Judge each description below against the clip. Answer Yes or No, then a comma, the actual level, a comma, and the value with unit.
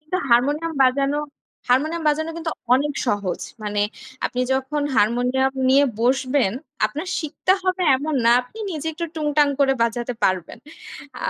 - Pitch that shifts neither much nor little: Yes, average, 3.8 semitones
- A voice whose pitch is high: Yes, very high, 275 Hz